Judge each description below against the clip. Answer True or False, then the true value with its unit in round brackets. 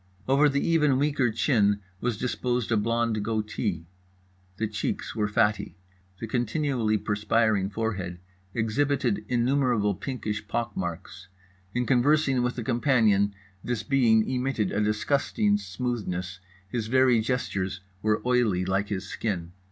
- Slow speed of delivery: True (130 wpm)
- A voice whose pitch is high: False (110 Hz)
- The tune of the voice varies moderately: True (3.4 semitones)